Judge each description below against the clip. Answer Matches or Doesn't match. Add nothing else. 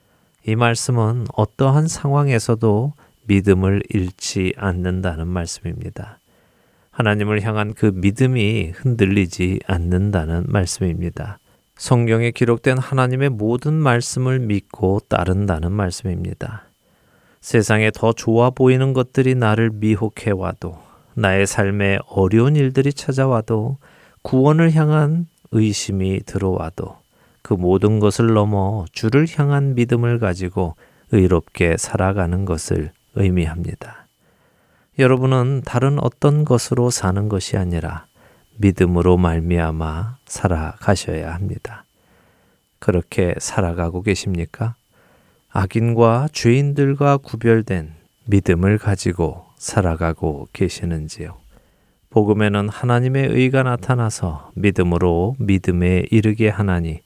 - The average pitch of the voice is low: Matches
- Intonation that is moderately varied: Matches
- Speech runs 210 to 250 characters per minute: Doesn't match